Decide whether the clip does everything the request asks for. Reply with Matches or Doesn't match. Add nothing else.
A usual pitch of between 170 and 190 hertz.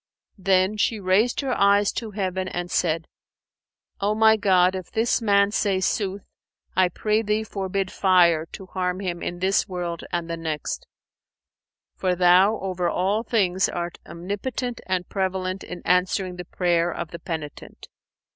Matches